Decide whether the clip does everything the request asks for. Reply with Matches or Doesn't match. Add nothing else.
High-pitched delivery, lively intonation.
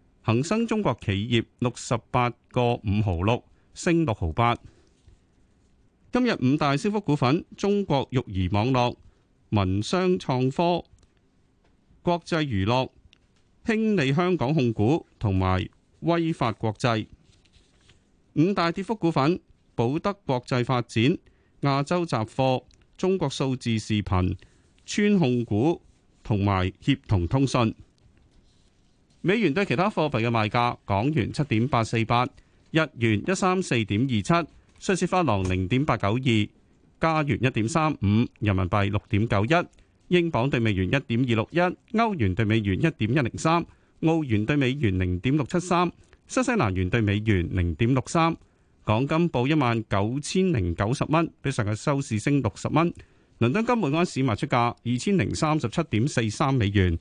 Doesn't match